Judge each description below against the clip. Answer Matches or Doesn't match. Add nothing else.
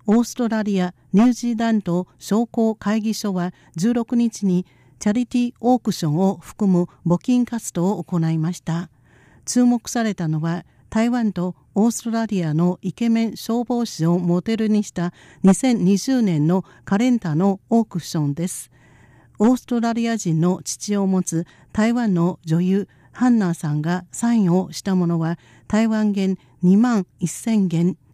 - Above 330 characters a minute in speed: Doesn't match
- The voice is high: Matches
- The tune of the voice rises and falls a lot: Doesn't match